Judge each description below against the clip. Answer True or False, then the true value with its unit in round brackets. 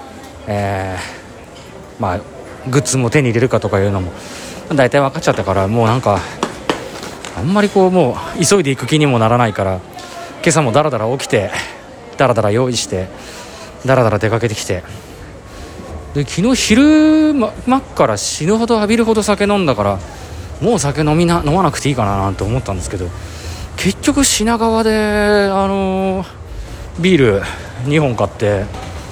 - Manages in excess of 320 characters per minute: False (305 characters per minute)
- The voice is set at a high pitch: False (125 Hz)